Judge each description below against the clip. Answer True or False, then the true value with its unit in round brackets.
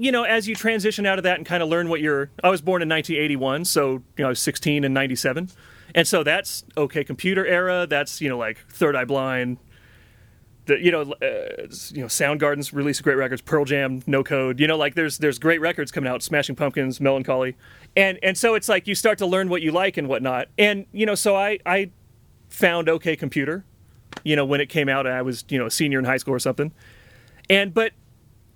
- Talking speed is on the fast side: True (230 wpm)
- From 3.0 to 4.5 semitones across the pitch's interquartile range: False (5.4 semitones)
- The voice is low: False (150 Hz)